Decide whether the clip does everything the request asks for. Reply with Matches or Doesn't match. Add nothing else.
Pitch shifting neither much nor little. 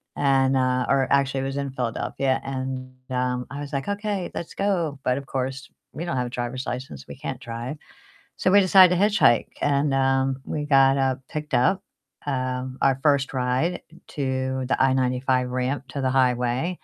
Doesn't match